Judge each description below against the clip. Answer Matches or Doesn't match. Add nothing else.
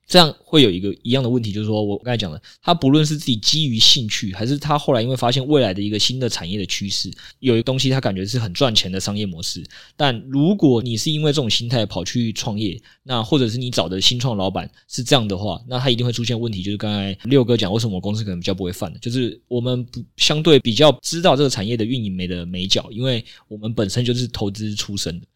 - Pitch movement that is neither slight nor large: Matches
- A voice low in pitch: Matches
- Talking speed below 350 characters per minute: Doesn't match